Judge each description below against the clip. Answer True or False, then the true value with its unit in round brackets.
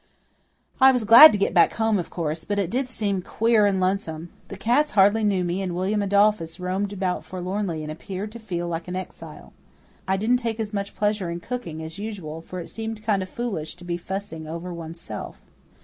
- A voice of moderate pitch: False (195 Hz)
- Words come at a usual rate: False (210 wpm)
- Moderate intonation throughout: True (3.7 semitones)